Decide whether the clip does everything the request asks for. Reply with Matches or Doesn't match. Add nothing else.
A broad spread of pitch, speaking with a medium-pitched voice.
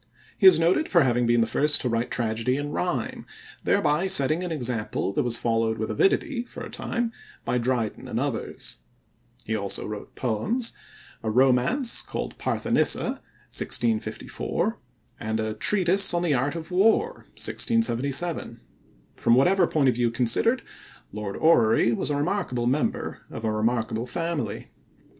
Doesn't match